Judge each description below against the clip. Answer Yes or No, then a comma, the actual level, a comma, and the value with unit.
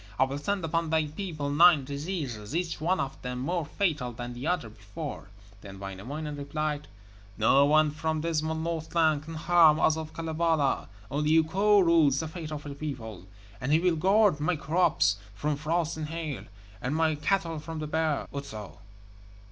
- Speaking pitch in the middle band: Yes, medium, 155 Hz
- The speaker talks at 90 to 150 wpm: No, average, 170 wpm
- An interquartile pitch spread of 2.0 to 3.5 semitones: Yes, average, 2.8 semitones